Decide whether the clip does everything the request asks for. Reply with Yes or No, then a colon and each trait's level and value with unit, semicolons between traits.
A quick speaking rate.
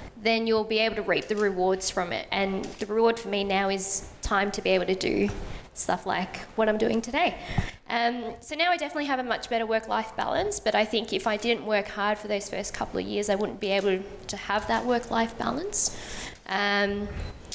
Yes: fast, 225 wpm